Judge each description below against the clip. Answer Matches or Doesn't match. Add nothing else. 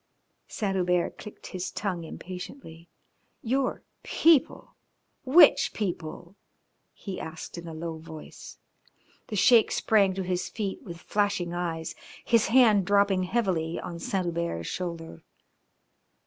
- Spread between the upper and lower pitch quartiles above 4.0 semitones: Doesn't match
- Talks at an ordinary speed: Doesn't match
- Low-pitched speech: Doesn't match